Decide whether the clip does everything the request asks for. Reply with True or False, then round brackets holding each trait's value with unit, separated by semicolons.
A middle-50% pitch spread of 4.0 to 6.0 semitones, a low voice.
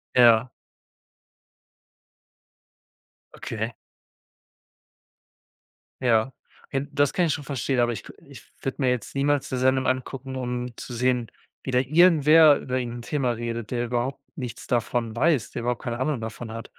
False (2.4 semitones; 125 Hz)